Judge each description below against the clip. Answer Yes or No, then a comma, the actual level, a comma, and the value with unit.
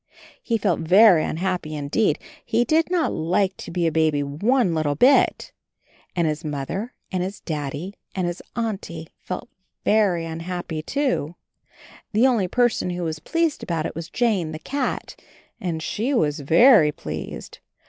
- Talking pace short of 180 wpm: Yes, average, 160 wpm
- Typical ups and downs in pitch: No, wide, 6.0 semitones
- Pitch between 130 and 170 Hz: No, medium, 180 Hz